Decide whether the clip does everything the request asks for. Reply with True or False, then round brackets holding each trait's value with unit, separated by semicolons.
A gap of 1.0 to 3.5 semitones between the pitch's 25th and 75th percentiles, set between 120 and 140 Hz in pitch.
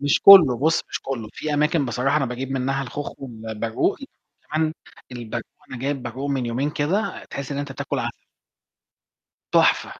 True (3.0 semitones; 135 Hz)